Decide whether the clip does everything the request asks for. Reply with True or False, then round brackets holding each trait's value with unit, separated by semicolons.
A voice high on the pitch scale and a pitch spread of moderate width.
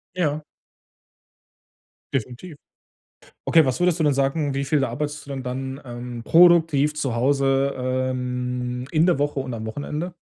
False (135 Hz; 3.1 semitones)